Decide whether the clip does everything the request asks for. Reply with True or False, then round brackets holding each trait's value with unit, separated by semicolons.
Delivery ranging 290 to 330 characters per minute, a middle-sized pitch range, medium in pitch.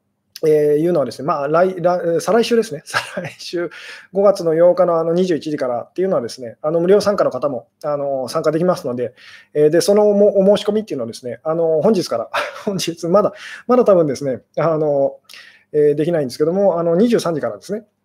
False (390 characters per minute; 4.9 semitones; 170 Hz)